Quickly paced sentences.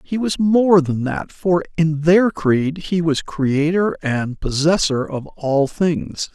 No: average, 160 wpm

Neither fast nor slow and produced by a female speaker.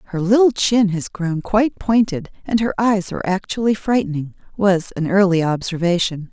Yes: average, 160 wpm; female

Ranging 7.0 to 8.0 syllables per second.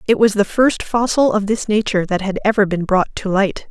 No: 5.5 syllables/s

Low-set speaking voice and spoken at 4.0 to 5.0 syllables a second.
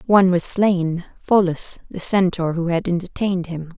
No: medium, 180 Hz; 4.7 syllables/s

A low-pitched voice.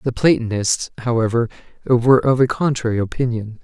Yes: low, 120 Hz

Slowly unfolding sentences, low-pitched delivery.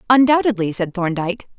No: slow, 115 wpm; high, 210 Hz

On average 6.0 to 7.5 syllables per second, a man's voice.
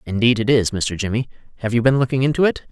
Yes: 6.7 syllables/s; male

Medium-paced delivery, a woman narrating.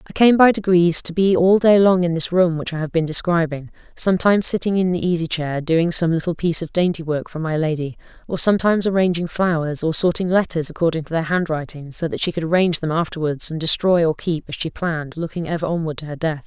No: fast, 235 wpm; female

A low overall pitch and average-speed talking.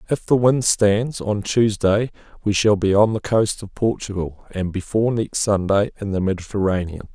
Yes: low, 105 Hz; average, 175 wpm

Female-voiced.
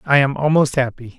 No: male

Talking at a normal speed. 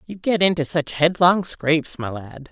Yes: average, 190 wpm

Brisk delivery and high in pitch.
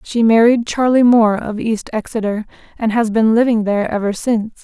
No: average, 180 wpm; high, 225 Hz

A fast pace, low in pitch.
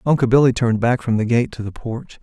Yes: fast, 270 wpm; low, 120 Hz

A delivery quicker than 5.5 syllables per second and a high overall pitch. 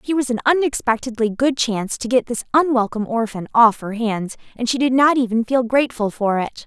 Yes: 5.8 syllables/s; high, 240 Hz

